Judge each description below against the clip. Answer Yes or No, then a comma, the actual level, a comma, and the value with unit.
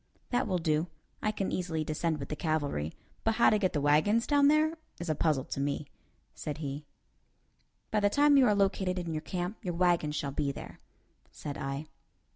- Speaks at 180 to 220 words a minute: Yes, average, 200 wpm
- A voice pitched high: No, medium, 170 Hz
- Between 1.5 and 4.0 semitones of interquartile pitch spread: No, wide, 5.6 semitones